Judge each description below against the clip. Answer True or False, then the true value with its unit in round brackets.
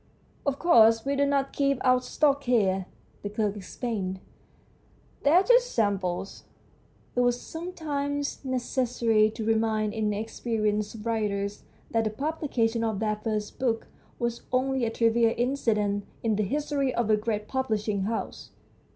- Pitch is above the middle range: True (230 Hz)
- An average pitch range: True (4.0 semitones)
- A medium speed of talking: True (145 wpm)